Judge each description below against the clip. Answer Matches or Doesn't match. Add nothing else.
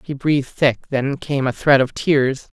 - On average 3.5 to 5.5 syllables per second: Matches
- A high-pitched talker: Doesn't match